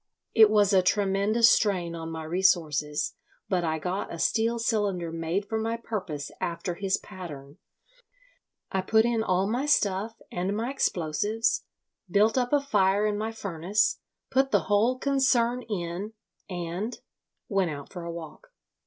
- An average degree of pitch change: Yes, average, 4.5 semitones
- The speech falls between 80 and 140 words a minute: No, average, 150 wpm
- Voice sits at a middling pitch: No, high, 195 Hz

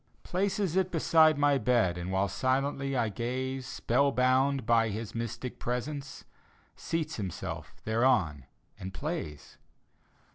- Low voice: Yes, low, 130 Hz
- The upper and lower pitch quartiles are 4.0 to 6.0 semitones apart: Yes, average, 4.3 semitones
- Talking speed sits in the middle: No, slow, 120 wpm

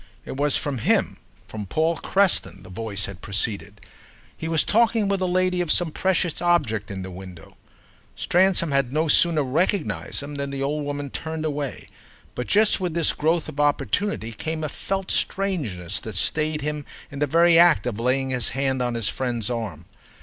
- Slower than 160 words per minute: No, average, 185 wpm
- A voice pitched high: No, medium, 145 Hz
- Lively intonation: Yes, wide, 6.5 semitones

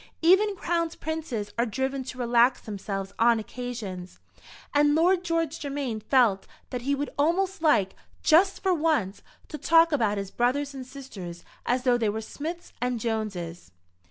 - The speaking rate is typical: Yes, average, 155 wpm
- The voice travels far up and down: Yes, wide, 6.5 semitones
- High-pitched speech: Yes, very high, 255 Hz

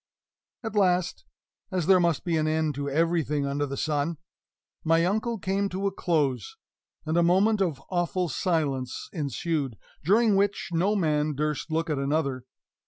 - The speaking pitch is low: No, medium, 165 Hz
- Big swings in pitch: No, average, 4.1 semitones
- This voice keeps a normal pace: Yes, average, 160 wpm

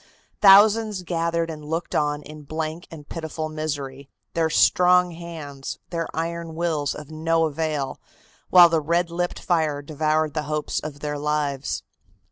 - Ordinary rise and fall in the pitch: No, narrow, 2.1 semitones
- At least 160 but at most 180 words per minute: No, average, 145 wpm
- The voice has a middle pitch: Yes, medium, 160 Hz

